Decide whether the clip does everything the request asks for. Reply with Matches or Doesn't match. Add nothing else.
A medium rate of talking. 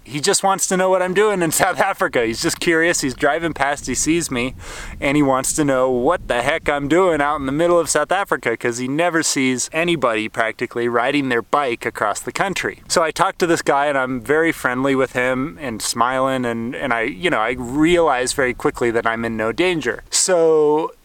Doesn't match